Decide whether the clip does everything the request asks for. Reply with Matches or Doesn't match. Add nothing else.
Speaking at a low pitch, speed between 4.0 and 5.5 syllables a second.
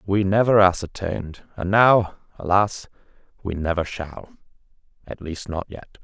Matches